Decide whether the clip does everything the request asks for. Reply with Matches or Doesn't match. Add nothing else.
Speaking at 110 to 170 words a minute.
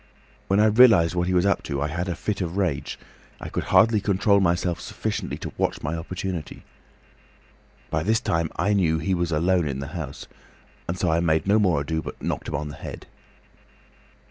Doesn't match